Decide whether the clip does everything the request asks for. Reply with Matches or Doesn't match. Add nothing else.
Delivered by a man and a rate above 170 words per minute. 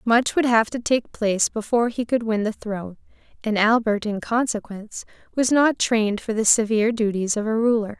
Doesn't match